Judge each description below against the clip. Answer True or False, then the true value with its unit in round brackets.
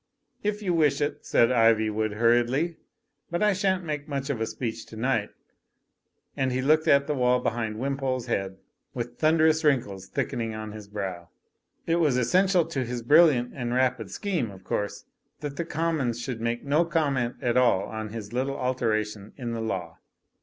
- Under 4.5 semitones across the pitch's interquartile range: False (5.0 semitones)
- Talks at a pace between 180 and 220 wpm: True (185 wpm)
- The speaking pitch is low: True (125 Hz)